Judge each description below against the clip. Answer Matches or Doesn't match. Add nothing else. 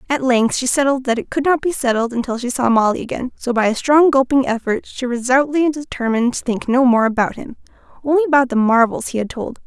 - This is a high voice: Matches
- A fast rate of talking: Matches